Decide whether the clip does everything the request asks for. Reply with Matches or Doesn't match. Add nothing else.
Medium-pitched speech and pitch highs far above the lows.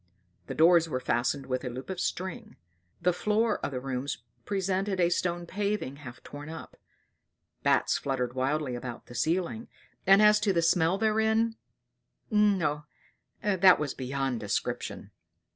Matches